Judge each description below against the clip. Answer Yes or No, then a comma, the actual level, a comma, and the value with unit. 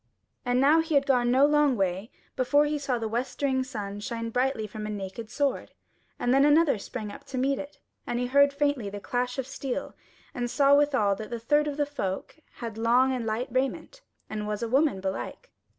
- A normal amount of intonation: Yes, average, 4.2 semitones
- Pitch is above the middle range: Yes, very high, 250 Hz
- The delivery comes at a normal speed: No, fast, 210 wpm